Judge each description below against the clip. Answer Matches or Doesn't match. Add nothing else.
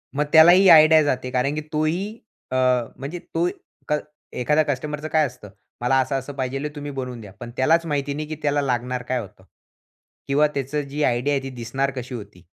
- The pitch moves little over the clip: Doesn't match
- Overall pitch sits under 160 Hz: Matches